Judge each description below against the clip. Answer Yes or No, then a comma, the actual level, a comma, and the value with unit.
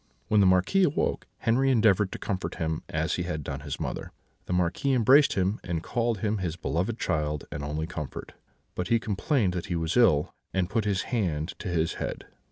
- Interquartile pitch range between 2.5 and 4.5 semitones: No, average, 5.3 semitones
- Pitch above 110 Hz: No, very low, 95 Hz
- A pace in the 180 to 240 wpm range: Yes, average, 200 wpm